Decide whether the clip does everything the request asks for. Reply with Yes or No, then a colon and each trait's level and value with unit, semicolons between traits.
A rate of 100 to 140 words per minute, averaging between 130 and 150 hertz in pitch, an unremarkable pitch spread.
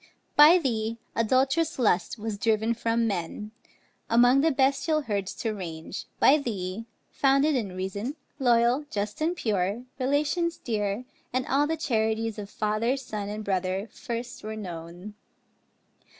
No: slow, 135 wpm; high, 225 Hz; average, 4.5 semitones